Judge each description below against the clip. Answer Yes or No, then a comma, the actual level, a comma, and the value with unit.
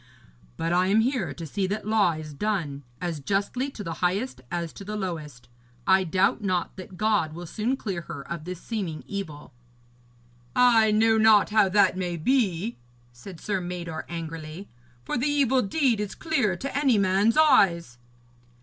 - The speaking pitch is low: No, high, 190 Hz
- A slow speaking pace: No, average, 170 wpm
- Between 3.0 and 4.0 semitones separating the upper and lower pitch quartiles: No, average, 4.4 semitones